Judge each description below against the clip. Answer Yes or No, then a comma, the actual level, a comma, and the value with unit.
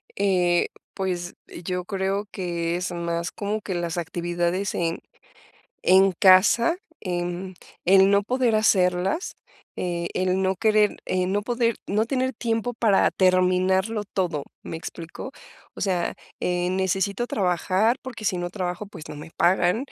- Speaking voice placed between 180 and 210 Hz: Yes, medium, 185 Hz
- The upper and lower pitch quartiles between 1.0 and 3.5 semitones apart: Yes, average, 2.8 semitones